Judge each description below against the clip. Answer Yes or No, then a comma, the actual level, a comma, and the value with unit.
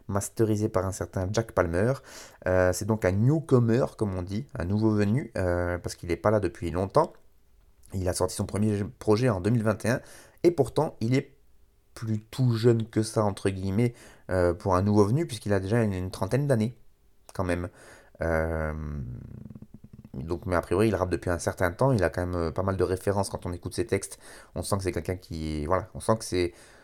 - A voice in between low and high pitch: No, low, 100 Hz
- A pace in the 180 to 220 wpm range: Yes, average, 205 wpm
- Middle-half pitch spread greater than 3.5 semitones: Yes, average, 3.9 semitones